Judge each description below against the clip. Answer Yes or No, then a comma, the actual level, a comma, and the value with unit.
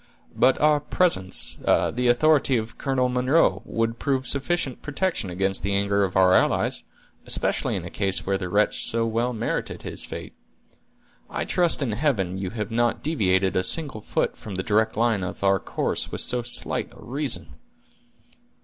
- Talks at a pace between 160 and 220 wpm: Yes, average, 165 wpm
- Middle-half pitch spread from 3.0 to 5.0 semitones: No, wide, 5.5 semitones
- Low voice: Yes, low, 115 Hz